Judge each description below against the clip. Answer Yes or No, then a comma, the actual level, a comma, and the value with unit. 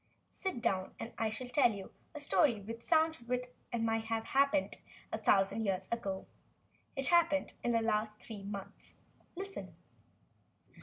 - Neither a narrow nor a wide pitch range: Yes, average, 4.7 semitones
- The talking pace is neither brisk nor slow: Yes, average, 160 wpm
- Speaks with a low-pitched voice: No, high, 230 Hz